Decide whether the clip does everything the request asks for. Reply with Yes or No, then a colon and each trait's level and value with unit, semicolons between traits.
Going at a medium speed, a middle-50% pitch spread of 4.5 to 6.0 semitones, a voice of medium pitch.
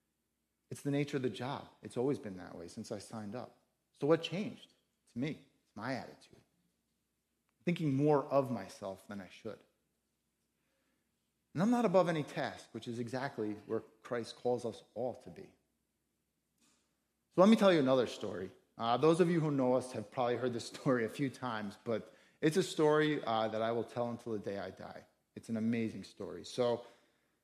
No: average, 190 wpm; average, 5.1 semitones; low, 125 Hz